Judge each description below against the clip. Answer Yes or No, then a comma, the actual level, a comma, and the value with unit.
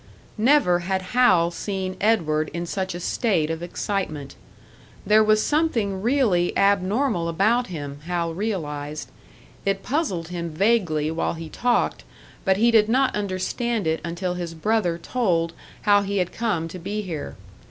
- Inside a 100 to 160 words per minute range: Yes, average, 150 wpm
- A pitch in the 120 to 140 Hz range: No, medium, 185 Hz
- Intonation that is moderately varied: Yes, average, 4.3 semitones